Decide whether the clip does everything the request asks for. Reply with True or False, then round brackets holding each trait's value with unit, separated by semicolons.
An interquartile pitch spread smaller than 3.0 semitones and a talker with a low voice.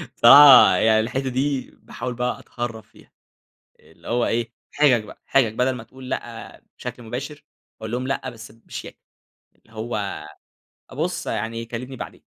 True (2.5 semitones; 120 Hz)